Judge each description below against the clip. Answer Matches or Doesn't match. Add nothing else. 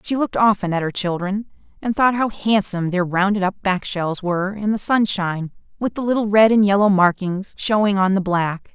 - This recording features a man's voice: Doesn't match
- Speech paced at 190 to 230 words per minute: Matches